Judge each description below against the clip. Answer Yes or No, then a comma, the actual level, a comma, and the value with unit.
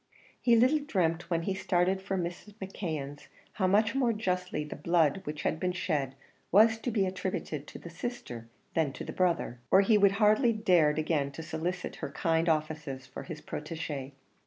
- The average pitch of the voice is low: No, medium, 175 Hz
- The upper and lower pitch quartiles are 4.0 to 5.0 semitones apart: Yes, average, 4.5 semitones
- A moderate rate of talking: Yes, average, 180 wpm